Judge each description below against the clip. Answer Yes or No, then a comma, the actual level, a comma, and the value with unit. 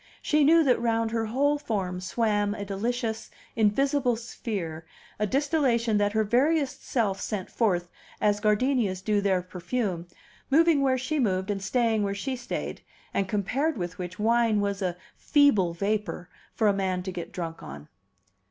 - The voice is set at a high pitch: Yes, high, 215 Hz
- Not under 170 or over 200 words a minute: No, average, 160 wpm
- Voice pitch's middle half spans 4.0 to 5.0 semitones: Yes, average, 4.5 semitones